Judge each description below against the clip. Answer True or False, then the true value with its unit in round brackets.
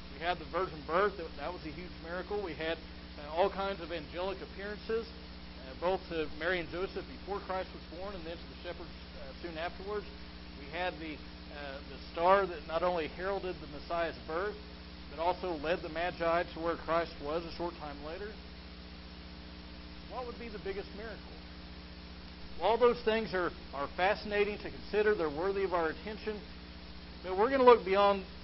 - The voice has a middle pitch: True (170 Hz)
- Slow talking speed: False (185 wpm)